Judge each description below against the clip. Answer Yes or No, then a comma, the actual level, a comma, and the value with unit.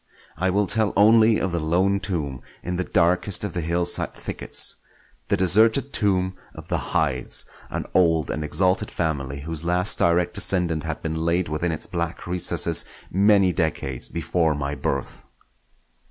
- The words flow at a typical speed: Yes, average, 155 wpm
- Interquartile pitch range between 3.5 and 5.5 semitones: No, average, 2.9 semitones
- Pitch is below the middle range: Yes, very low, 85 Hz